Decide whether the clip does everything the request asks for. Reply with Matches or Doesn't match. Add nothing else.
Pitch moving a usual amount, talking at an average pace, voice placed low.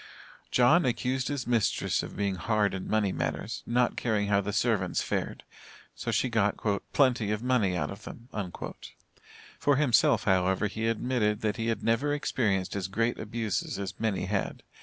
Matches